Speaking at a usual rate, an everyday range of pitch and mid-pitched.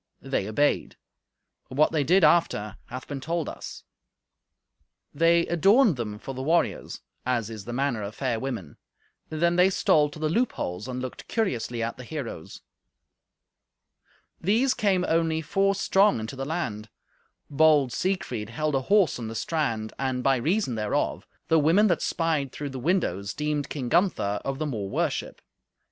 No: average, 160 wpm; wide, 6.1 semitones; medium, 145 Hz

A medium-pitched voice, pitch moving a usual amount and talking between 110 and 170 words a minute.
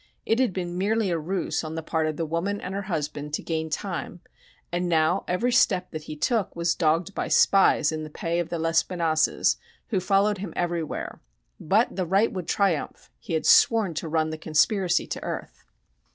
No: medium, 175 Hz; average, 3.5 semitones; average, 195 wpm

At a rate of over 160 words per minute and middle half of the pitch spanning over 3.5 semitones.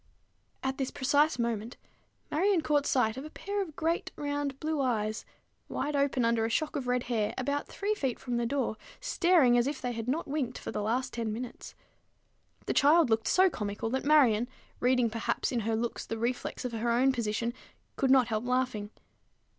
Yes: average, 195 wpm; average, 3.9 semitones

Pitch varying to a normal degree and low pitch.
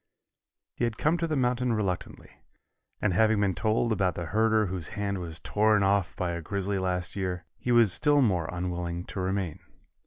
Yes: average, 3.6 semitones; low, 100 Hz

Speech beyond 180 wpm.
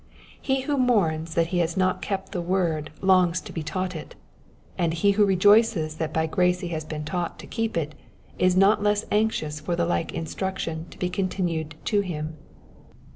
Yes: average, 190 wpm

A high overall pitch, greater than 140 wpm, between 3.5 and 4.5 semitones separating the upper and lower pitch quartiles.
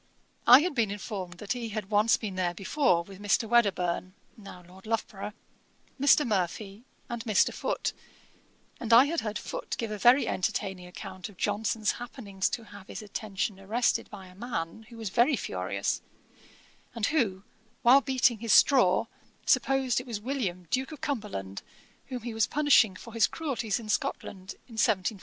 Yes: high, 215 Hz; average, 170 wpm; average, 4.1 semitones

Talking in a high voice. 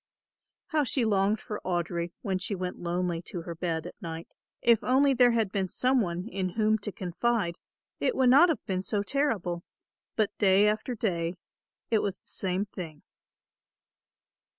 Yes: high, 195 Hz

